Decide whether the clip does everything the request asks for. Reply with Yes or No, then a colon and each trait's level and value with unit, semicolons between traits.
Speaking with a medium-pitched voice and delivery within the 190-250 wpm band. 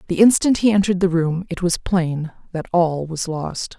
Yes: medium, 175 Hz; fast, 205 wpm